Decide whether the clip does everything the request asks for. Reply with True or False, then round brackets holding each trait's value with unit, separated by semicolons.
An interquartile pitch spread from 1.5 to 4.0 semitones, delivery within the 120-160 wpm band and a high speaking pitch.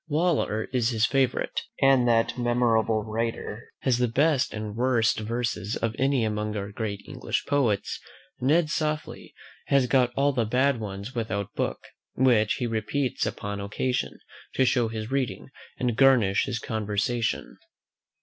False (3.3 semitones; 150 wpm; 120 Hz)